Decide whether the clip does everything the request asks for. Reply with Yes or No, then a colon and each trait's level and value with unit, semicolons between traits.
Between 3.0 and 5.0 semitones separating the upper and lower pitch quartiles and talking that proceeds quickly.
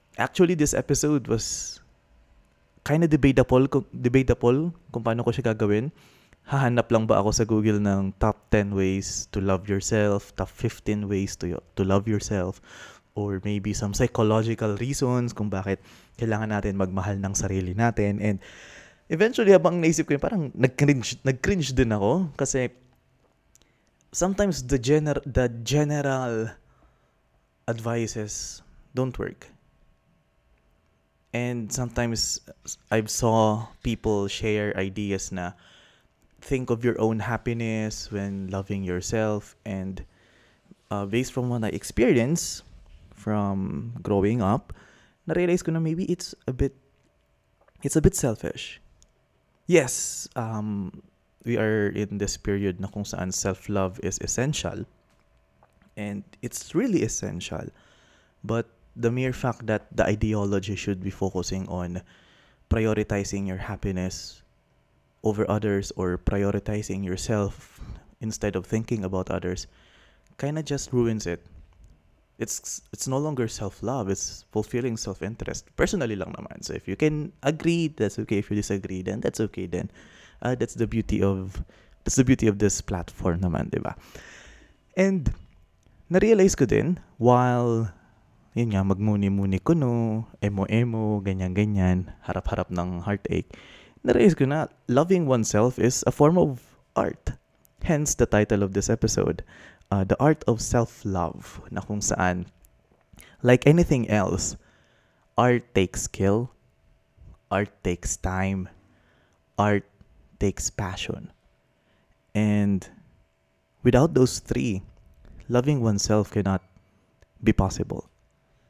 No: average, 4.2 semitones; average, 125 wpm